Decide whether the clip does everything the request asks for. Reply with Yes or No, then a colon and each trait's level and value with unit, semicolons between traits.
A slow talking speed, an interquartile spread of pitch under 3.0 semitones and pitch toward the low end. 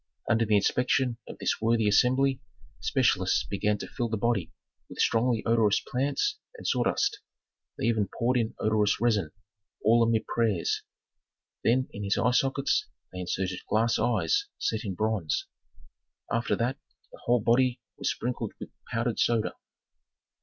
No: average, 145 wpm; narrow, 2.6 semitones; low, 115 Hz